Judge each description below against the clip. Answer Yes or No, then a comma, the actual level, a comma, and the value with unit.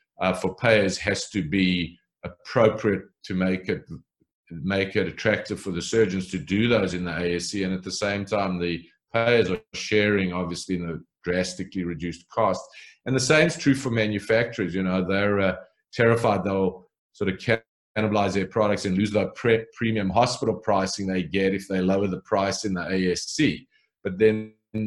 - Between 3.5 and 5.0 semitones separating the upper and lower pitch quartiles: No, average, 2.8 semitones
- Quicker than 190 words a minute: No, average, 180 wpm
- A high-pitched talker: No, low, 100 Hz